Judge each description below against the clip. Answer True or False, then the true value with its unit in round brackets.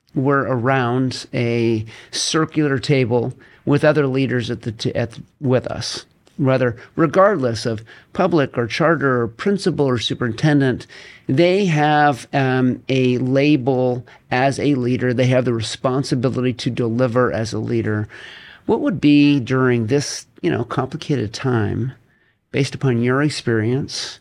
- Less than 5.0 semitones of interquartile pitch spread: True (2.9 semitones)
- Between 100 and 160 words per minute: True (135 wpm)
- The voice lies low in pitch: True (130 Hz)